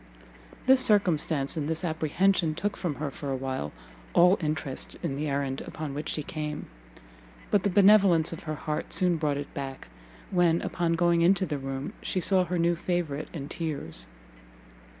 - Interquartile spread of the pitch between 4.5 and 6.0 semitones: No, average, 3.6 semitones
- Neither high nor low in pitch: Yes, medium, 160 Hz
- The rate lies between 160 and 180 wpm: Yes, average, 170 wpm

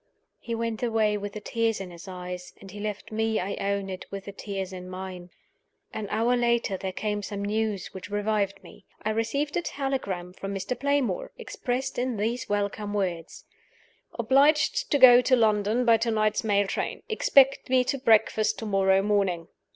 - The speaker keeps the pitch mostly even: No, average, 3.3 semitones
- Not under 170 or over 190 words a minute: Yes, average, 180 wpm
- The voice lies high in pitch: Yes, high, 210 Hz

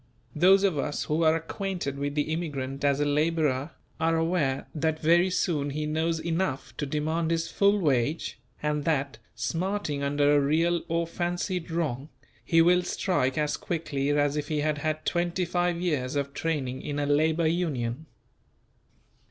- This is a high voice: No, medium, 155 Hz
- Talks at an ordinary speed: Yes, average, 165 wpm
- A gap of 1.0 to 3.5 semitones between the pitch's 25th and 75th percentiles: Yes, average, 2.8 semitones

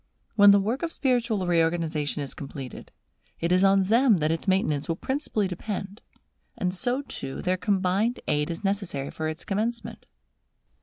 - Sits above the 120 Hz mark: Yes, high, 190 Hz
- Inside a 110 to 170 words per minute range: Yes, average, 160 wpm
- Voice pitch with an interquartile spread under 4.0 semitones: No, average, 4.8 semitones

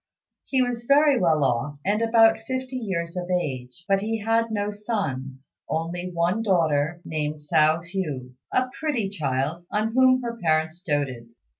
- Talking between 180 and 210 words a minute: No, average, 155 wpm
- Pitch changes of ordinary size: No, wide, 6.7 semitones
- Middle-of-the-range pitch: Yes, medium, 180 Hz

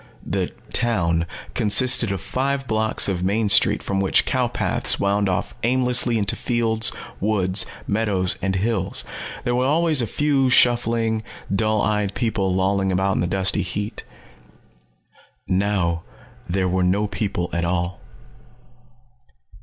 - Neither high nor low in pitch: No, low, 105 Hz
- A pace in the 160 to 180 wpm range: No, slow, 135 wpm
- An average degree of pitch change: Yes, average, 3.8 semitones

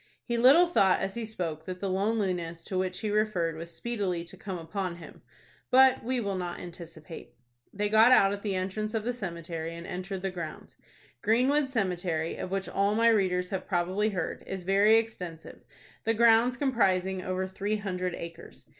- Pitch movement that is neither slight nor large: Yes, average, 3.6 semitones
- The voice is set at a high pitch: Yes, high, 195 Hz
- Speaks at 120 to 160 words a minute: No, average, 180 wpm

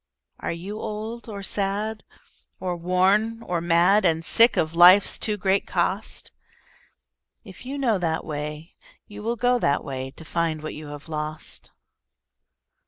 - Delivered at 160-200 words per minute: No, average, 150 wpm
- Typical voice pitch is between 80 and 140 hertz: No, medium, 185 Hz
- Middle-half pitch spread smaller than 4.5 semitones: No, average, 4.8 semitones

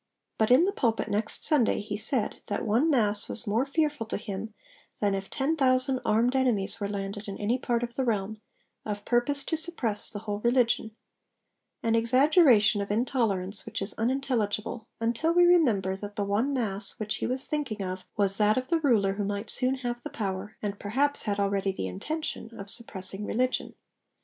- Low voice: No, high, 225 Hz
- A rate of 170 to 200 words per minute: Yes, average, 190 wpm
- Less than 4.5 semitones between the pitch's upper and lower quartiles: Yes, average, 4.0 semitones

